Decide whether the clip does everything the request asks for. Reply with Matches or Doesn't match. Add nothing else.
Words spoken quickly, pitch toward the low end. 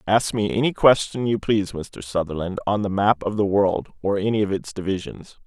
Matches